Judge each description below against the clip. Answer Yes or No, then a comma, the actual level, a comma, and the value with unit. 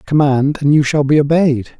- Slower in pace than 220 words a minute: Yes, average, 200 wpm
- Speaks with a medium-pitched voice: Yes, medium, 145 Hz